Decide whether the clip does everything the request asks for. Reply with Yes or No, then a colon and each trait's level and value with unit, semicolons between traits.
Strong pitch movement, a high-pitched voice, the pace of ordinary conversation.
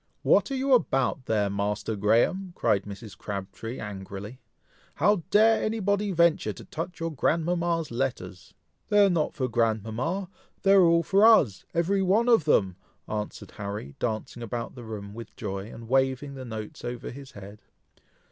No: wide, 8.8 semitones; low, 130 Hz; average, 165 wpm